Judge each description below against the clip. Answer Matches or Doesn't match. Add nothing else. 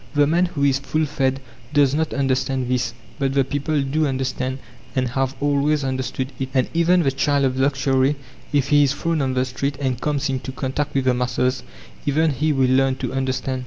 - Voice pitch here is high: Doesn't match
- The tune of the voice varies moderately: Doesn't match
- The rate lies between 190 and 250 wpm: Matches